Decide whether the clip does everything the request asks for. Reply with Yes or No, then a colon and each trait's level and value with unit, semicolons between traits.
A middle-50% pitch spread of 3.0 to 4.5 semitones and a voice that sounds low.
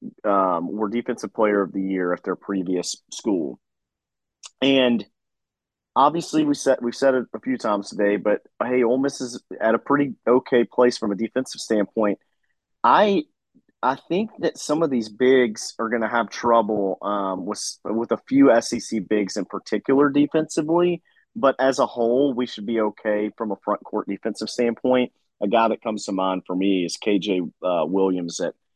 Yes: average, 4.1 semitones; low, 115 Hz